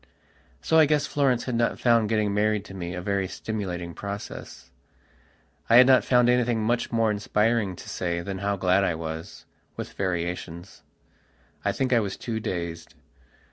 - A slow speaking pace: No, average, 170 wpm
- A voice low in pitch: Yes, low, 105 Hz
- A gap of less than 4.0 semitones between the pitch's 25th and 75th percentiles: No, average, 4.5 semitones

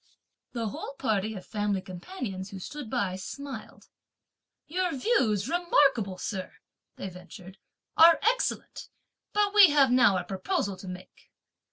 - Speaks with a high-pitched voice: Yes, high, 215 Hz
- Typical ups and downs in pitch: No, wide, 7.5 semitones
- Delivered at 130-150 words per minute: Yes, slow, 135 wpm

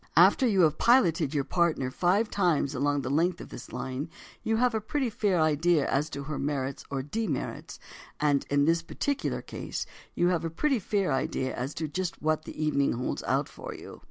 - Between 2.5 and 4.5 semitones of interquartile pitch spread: No, average, 4.9 semitones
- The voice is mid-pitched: Yes, medium, 155 Hz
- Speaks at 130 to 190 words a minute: No, average, 200 wpm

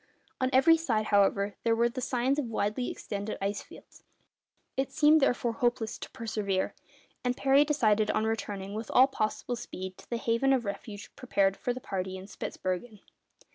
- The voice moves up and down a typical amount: Yes, average, 4.0 semitones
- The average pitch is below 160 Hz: No, high, 225 Hz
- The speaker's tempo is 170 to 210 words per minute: Yes, average, 175 wpm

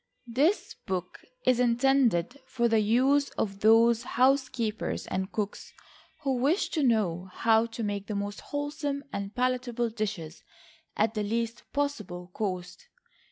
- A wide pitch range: No, average, 4.2 semitones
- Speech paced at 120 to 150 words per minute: Yes, slow, 135 wpm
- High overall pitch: Yes, high, 230 Hz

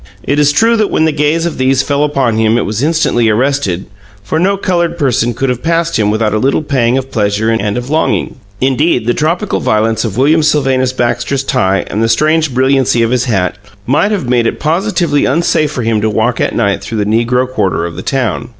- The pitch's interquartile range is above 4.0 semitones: Yes, average, 5.0 semitones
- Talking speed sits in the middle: No, fast, 220 wpm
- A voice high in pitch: No, low, 130 Hz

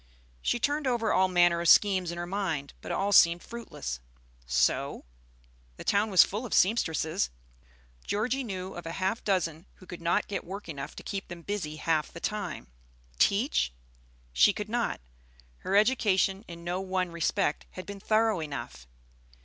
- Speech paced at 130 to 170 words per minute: Yes, average, 165 wpm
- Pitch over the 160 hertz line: Yes, medium, 185 Hz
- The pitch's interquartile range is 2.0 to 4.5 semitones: Yes, average, 3.7 semitones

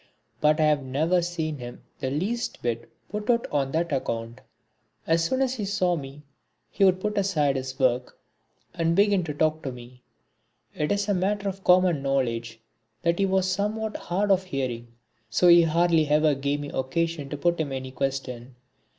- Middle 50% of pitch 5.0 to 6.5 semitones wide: Yes, wide, 5.6 semitones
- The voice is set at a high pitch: No, medium, 155 Hz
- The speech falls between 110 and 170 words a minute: No, average, 185 wpm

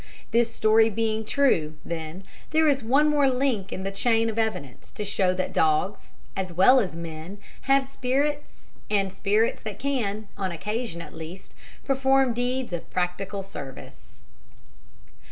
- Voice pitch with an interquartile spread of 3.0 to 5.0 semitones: No, wide, 5.5 semitones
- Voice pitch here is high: Yes, high, 215 Hz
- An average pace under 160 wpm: Yes, average, 150 wpm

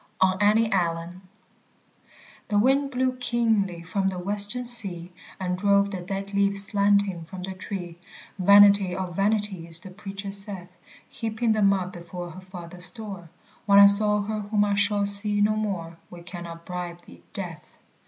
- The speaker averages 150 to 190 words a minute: Yes, average, 160 wpm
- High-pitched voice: Yes, high, 200 Hz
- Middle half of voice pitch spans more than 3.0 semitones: No, narrow, 2.4 semitones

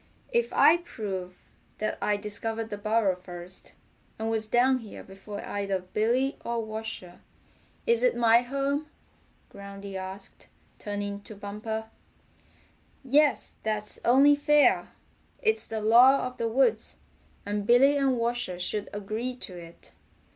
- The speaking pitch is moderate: No, high, 220 Hz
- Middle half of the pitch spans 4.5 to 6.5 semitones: No, average, 4.0 semitones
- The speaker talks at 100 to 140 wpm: Yes, slow, 135 wpm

